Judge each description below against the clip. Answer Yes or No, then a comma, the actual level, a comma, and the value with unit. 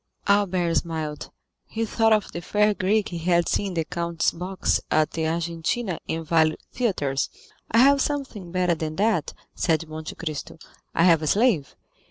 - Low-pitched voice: No, medium, 170 Hz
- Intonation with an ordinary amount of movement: Yes, average, 4.4 semitones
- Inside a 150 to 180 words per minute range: Yes, average, 170 wpm